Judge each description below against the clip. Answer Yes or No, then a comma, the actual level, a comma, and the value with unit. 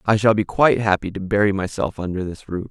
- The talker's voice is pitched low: Yes, low, 100 Hz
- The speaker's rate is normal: No, fast, 245 wpm